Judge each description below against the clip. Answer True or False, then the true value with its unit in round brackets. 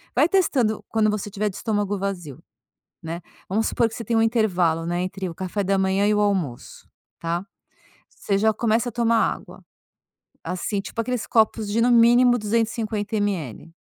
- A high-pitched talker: True (210 Hz)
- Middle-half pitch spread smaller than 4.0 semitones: True (3.2 semitones)